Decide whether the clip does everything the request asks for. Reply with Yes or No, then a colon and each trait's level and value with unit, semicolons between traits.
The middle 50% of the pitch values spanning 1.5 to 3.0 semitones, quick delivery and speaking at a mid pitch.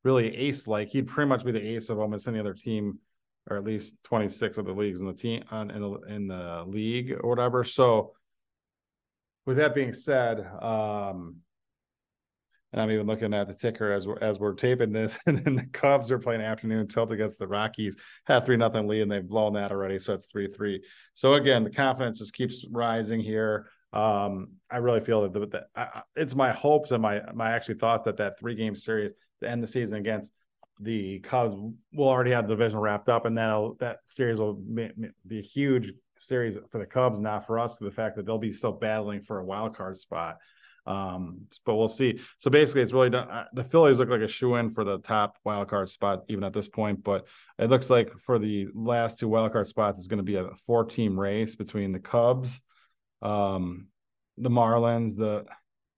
No: narrow, 2.5 semitones; fast, 210 wpm; low, 110 Hz